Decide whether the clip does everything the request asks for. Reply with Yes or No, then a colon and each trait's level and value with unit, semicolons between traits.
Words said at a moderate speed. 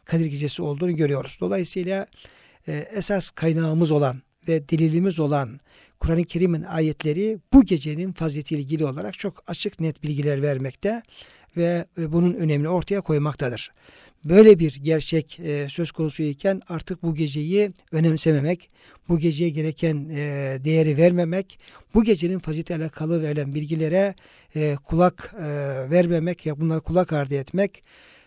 Yes: average, 120 wpm